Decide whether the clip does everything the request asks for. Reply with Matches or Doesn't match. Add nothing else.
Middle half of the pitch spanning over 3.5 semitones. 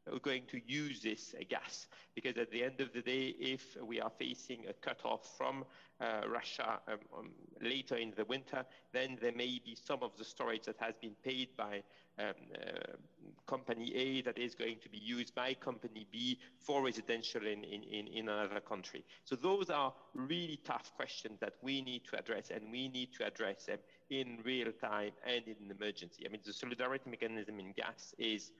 Doesn't match